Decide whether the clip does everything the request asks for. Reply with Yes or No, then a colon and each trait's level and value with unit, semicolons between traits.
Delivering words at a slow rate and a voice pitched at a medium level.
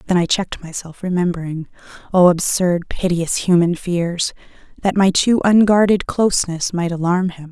Yes: slow, 130 wpm; medium, 180 Hz